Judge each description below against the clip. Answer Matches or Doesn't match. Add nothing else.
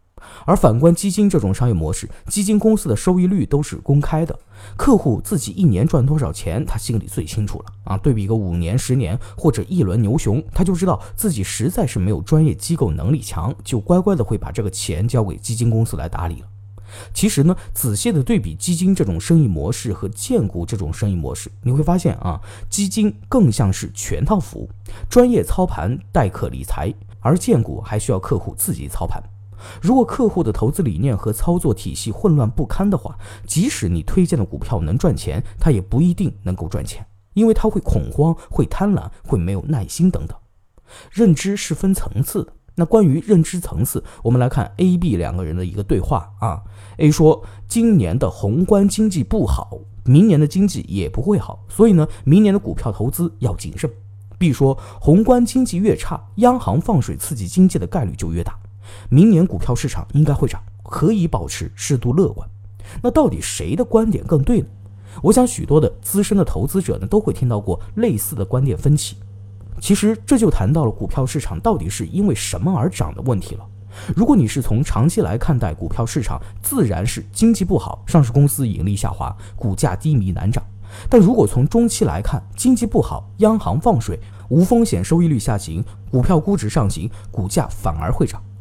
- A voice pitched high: Doesn't match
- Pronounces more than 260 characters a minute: Matches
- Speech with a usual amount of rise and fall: Doesn't match